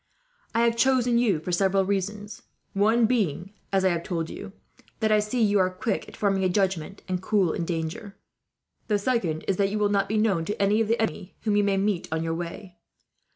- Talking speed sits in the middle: No, fast, 220 wpm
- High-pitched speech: Yes, high, 200 Hz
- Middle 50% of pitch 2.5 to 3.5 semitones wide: Yes, average, 2.8 semitones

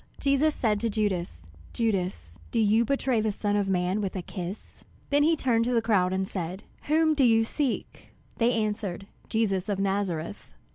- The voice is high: Yes, high, 210 Hz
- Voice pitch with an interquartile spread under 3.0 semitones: No, average, 3.7 semitones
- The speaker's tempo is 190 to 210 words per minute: No, average, 180 wpm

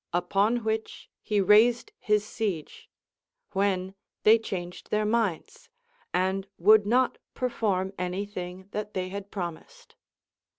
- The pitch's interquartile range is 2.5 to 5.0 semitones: Yes, average, 2.9 semitones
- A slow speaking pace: Yes, slow, 125 wpm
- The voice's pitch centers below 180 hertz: No, high, 205 Hz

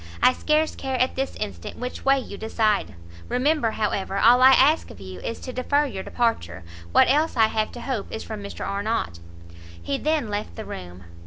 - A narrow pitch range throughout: No, average, 5.0 semitones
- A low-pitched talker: No, high, 225 Hz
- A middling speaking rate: Yes, average, 195 wpm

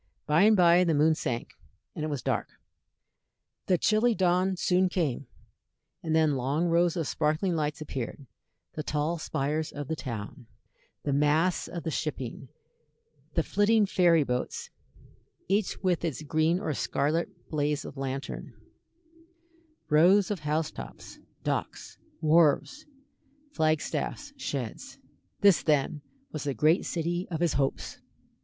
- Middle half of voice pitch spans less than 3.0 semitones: No, average, 3.3 semitones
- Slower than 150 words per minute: Yes, slow, 135 wpm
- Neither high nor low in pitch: Yes, medium, 160 Hz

